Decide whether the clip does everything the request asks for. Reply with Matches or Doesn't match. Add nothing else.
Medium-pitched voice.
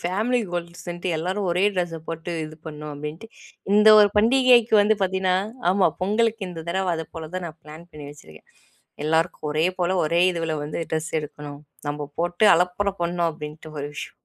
Matches